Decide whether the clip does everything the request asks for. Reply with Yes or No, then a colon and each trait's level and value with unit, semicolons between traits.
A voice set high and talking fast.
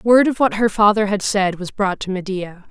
Yes: high, 205 Hz; fast, 245 wpm